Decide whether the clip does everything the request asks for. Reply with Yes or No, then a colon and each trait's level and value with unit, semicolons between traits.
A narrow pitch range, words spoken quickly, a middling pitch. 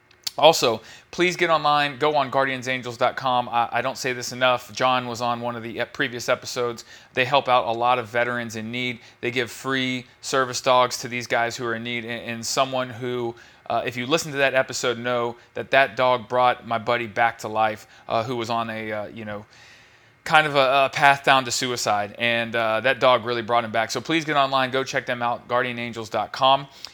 No: narrow, 2.0 semitones; fast, 215 wpm; low, 125 Hz